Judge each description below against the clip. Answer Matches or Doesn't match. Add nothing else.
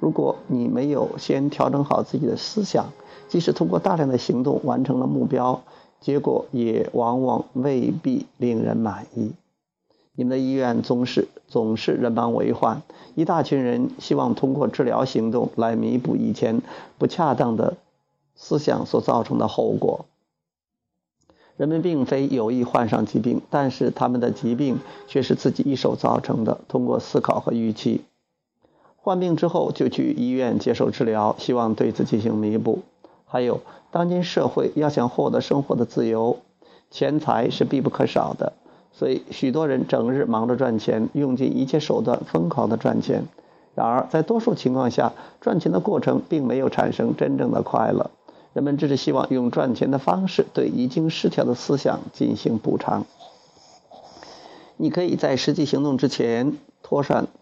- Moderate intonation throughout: Matches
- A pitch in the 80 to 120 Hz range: Doesn't match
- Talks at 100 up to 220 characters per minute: Doesn't match